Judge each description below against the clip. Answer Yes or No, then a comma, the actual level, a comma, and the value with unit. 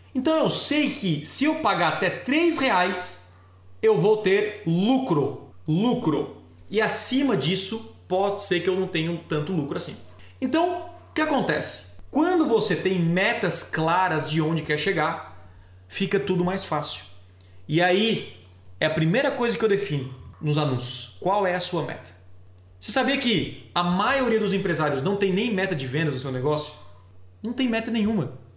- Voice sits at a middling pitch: Yes, medium, 180 Hz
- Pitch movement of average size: No, wide, 6.6 semitones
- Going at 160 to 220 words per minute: Yes, average, 170 wpm